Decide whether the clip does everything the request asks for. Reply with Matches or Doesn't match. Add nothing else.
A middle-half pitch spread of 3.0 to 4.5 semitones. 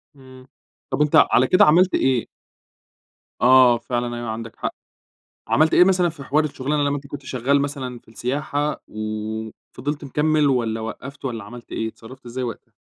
Matches